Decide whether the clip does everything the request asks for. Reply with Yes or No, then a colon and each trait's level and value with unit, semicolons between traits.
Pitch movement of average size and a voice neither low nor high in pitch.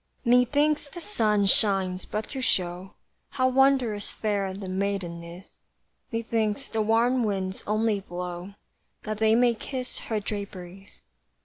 No: average, 3.8 semitones; high, 210 Hz